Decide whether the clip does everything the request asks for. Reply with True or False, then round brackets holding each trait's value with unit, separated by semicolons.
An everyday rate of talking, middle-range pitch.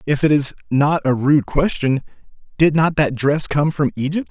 True (195 wpm; 145 Hz)